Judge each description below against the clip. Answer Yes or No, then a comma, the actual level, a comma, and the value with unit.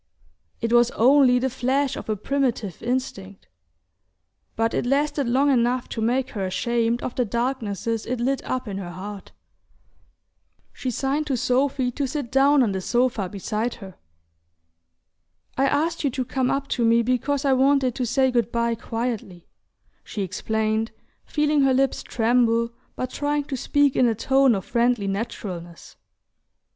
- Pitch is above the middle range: Yes, high, 245 Hz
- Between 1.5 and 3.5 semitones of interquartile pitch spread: Yes, average, 3.1 semitones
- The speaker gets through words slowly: No, average, 160 wpm